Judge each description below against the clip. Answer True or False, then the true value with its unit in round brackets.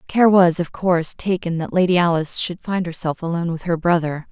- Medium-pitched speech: True (170 Hz)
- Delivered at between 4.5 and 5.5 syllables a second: False (5.8 syllables/s)